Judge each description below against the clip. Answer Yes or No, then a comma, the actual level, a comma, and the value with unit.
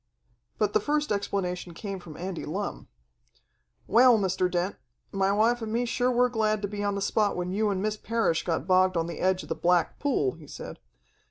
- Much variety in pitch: No, average, 3.6 semitones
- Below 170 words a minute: No, fast, 205 wpm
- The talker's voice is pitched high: Yes, high, 200 Hz